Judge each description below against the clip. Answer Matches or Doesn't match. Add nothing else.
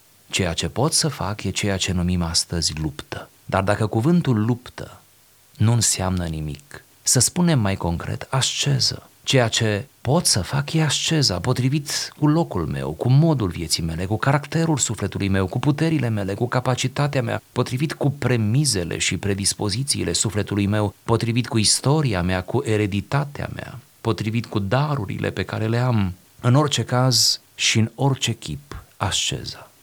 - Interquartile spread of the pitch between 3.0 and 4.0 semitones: Doesn't match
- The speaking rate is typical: Matches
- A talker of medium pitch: Doesn't match